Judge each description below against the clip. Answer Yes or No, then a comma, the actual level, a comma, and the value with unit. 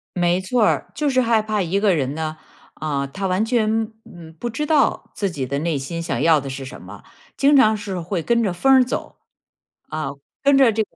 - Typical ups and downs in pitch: No, wide, 6.5 semitones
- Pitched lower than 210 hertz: Yes, high, 195 Hz